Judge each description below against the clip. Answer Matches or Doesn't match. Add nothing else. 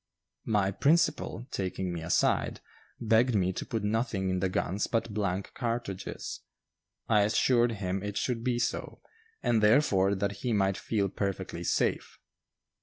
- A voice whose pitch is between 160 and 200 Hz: Doesn't match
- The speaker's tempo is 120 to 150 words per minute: Matches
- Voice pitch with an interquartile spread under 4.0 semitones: Matches